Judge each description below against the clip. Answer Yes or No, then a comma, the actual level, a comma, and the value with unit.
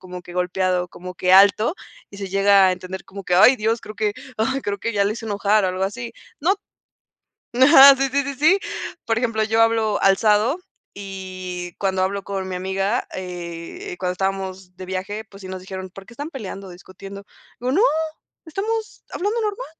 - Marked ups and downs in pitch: No, average, 3.6 semitones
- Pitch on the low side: No, high, 200 Hz